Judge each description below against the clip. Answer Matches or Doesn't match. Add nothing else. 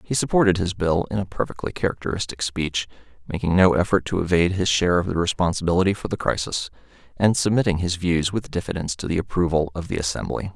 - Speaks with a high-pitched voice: Doesn't match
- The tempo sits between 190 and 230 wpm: Matches